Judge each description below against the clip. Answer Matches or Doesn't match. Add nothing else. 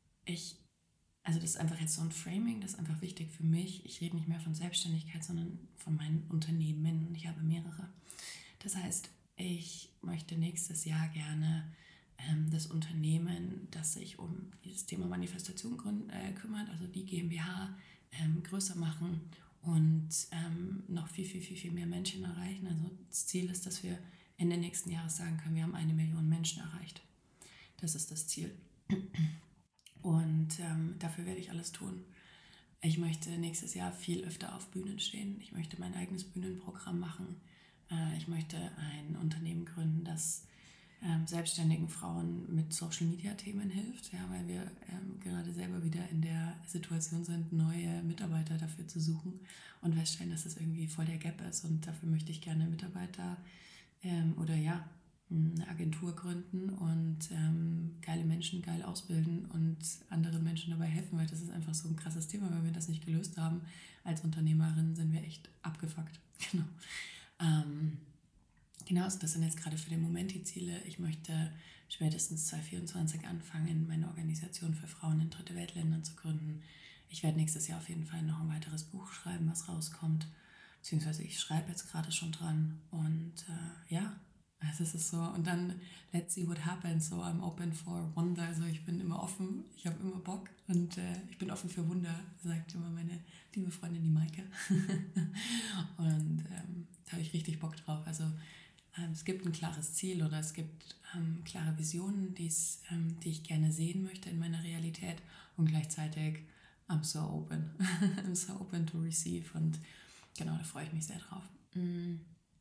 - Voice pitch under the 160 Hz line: Doesn't match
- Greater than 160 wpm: Matches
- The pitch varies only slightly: Matches